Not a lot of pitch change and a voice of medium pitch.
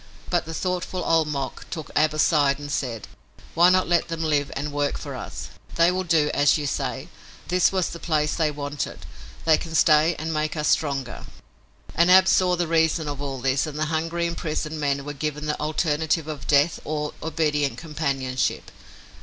Yes: narrow, 2.3 semitones; medium, 155 Hz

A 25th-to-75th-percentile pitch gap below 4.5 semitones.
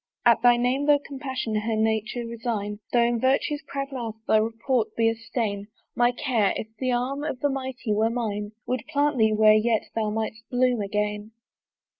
Yes: average, 3.0 semitones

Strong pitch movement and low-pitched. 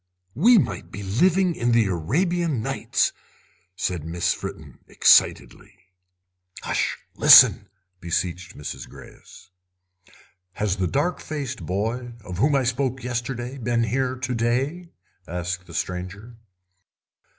Yes: wide, 6.8 semitones; low, 120 Hz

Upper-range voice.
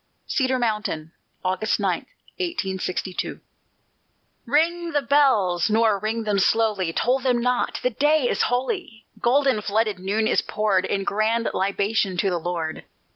Yes: high, 220 Hz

